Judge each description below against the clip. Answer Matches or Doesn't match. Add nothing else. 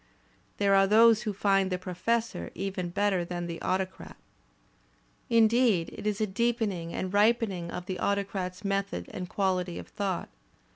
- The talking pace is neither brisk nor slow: Matches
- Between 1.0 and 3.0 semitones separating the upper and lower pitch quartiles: Matches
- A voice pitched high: Matches